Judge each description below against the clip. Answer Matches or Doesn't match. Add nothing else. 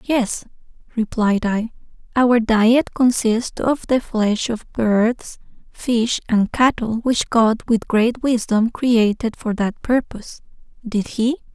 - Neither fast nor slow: Doesn't match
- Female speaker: Matches